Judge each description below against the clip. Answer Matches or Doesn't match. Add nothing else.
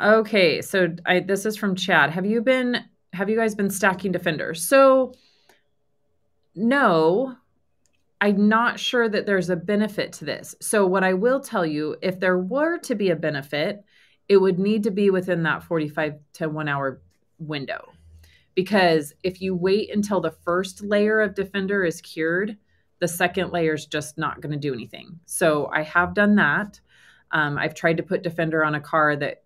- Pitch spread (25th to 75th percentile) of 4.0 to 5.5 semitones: Matches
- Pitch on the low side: Doesn't match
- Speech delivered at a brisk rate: Doesn't match